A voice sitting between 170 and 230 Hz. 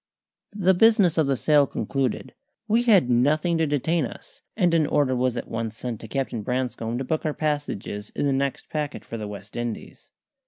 No: medium, 140 Hz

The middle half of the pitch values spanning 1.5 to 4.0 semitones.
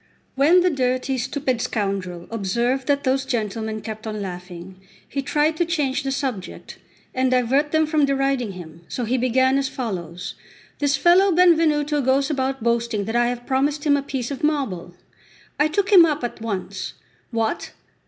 No: average, 4.5 semitones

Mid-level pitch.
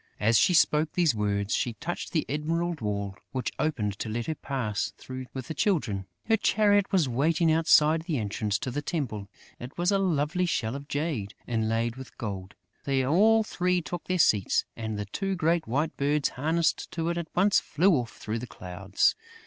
Yes: medium, 145 Hz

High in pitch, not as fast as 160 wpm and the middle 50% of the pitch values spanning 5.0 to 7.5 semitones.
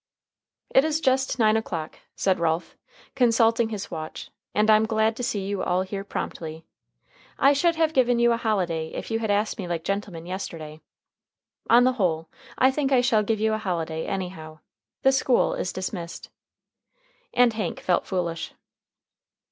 No: high, 210 Hz; average, 165 wpm; wide, 5.5 semitones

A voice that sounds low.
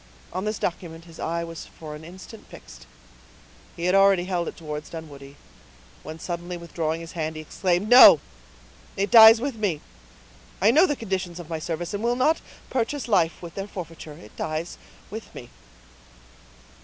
No: medium, 175 Hz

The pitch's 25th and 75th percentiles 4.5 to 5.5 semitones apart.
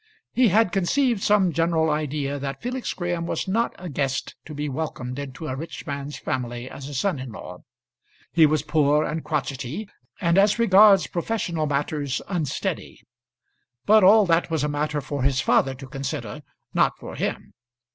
Yes: average, 4.8 semitones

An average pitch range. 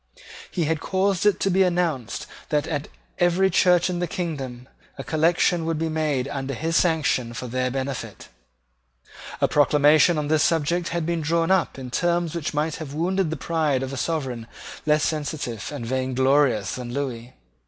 Yes: average, 4.2 semitones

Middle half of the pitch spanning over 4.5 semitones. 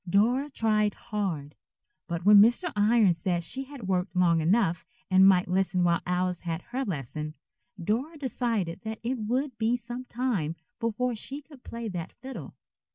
Yes: wide, 5.5 semitones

